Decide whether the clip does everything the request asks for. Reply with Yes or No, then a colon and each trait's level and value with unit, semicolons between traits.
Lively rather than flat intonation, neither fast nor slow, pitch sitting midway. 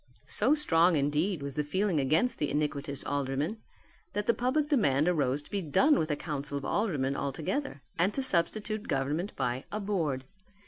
Yes: wide, 6.6 semitones; average, 175 wpm; medium, 155 Hz